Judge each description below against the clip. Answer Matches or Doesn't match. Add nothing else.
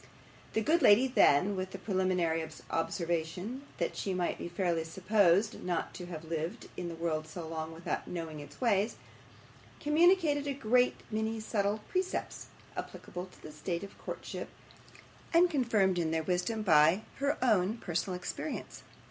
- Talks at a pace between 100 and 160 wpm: Matches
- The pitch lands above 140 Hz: Matches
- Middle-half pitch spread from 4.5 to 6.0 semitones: Matches